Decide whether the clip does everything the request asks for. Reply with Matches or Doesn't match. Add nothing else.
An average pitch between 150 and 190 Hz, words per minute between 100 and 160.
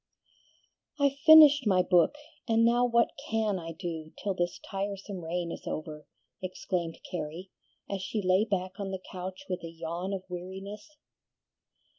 Matches